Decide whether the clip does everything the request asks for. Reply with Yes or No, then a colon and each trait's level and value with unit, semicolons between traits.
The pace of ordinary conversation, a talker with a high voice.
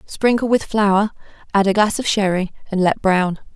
Yes: average, 185 wpm; high, 200 Hz